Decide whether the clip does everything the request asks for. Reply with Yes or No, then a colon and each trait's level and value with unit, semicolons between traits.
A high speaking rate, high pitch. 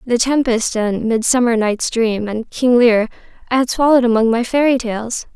No: average, 180 wpm; high, 235 Hz